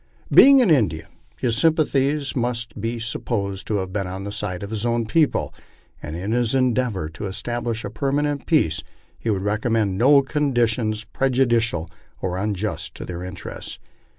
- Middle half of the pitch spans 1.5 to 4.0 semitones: No, average, 4.7 semitones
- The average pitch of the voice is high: No, low, 115 Hz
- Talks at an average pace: Yes, average, 160 wpm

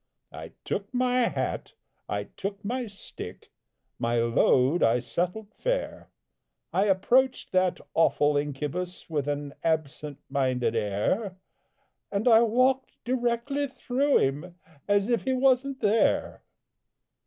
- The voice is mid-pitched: No, high, 195 Hz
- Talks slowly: Yes, slow, 120 wpm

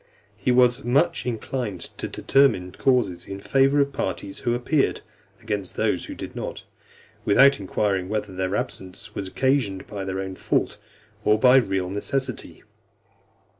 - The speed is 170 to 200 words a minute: No, average, 150 wpm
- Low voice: Yes, low, 105 Hz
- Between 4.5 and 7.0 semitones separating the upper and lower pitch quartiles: Yes, wide, 5.5 semitones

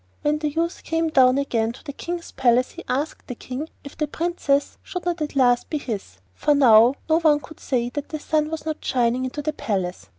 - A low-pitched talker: No, very high, 285 Hz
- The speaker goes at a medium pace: No, fast, 225 wpm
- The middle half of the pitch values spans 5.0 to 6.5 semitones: No, average, 3.8 semitones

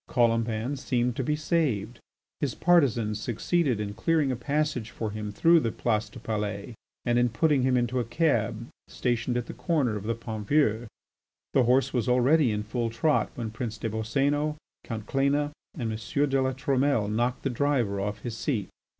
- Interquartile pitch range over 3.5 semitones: Yes, average, 4.0 semitones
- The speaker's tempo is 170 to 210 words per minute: Yes, average, 185 wpm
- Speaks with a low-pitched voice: Yes, low, 120 Hz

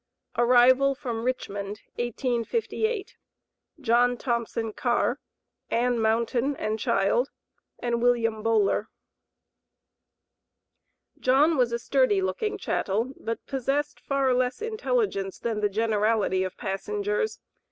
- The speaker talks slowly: Yes, slow, 100 wpm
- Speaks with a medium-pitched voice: No, high, 240 Hz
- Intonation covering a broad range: No, average, 3.5 semitones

